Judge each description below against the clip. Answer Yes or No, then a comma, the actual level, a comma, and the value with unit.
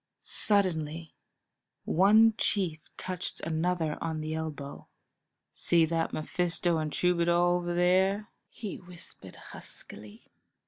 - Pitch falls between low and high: Yes, medium, 175 Hz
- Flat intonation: Yes, narrow, 2.3 semitones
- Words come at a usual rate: No, slow, 100 wpm